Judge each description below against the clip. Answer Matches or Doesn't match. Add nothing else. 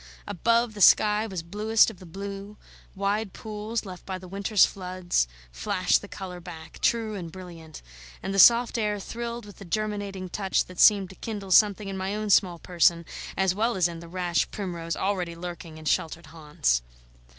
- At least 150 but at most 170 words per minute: Doesn't match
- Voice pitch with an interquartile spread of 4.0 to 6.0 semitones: Doesn't match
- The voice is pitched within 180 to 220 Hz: Matches